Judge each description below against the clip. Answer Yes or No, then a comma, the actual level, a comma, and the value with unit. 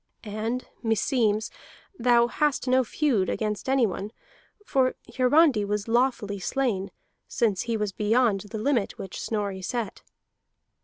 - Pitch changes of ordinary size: Yes, average, 3.6 semitones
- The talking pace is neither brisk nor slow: No, slow, 120 wpm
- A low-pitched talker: No, high, 225 Hz